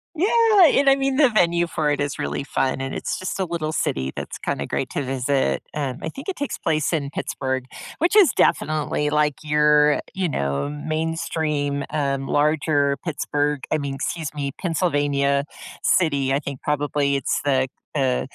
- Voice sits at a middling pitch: Yes, medium, 150 Hz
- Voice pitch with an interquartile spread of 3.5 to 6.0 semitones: No, average, 2.8 semitones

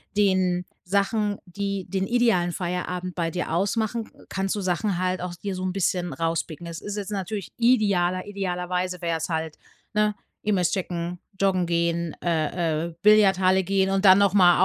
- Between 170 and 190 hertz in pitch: Yes, medium, 185 Hz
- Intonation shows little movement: Yes, narrow, 2.3 semitones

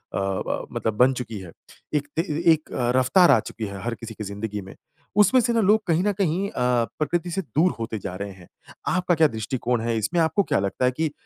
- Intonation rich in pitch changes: Yes, wide, 8.1 semitones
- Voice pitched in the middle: No, low, 125 Hz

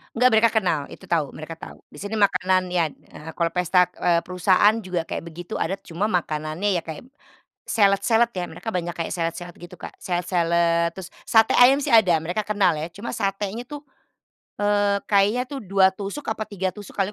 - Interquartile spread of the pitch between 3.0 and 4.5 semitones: Yes, average, 3.4 semitones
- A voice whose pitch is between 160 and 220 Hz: Yes, high, 190 Hz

